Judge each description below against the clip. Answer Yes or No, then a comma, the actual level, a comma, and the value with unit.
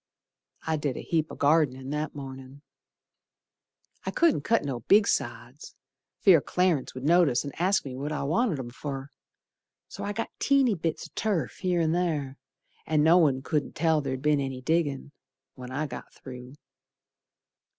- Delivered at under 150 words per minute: No, average, 165 wpm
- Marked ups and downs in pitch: No, average, 4.2 semitones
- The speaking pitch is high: No, medium, 150 Hz